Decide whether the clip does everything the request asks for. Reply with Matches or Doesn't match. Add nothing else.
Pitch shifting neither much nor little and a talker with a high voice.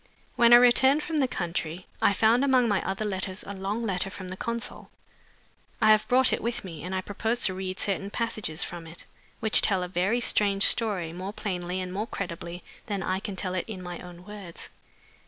Matches